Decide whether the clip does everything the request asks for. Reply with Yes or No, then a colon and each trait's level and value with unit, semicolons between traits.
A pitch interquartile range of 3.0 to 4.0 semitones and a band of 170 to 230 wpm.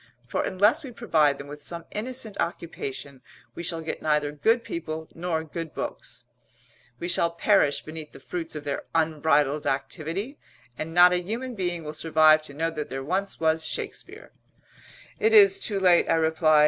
Yes: average, 3.5 semitones; average, 175 wpm